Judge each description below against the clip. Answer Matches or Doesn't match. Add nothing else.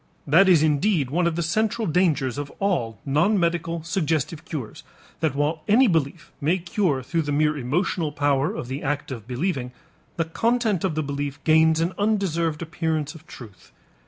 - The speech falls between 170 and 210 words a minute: Matches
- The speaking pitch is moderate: Matches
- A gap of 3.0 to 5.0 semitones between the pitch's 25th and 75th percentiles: Matches